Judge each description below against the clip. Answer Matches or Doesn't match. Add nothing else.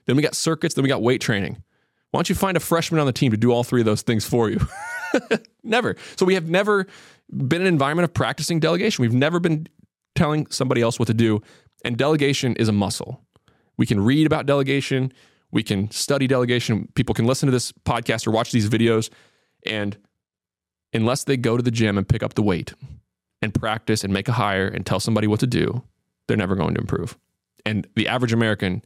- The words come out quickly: Matches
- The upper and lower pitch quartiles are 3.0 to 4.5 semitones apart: Doesn't match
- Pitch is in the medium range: Doesn't match